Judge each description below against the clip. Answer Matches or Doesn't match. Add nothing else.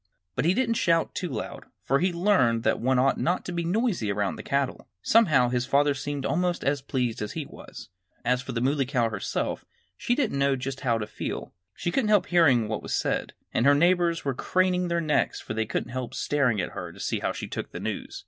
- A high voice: Doesn't match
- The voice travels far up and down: Matches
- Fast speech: Matches